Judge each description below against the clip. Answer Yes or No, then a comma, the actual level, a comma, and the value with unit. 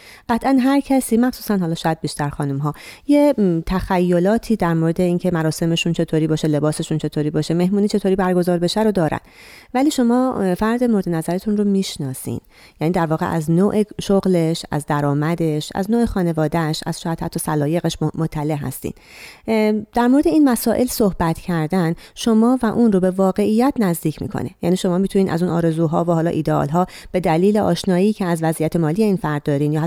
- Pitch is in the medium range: Yes, medium, 175 Hz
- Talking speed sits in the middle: No, fast, 170 wpm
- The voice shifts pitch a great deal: No, average, 4.5 semitones